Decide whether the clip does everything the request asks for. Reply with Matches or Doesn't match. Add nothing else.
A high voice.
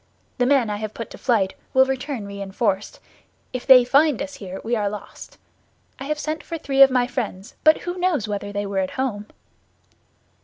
Matches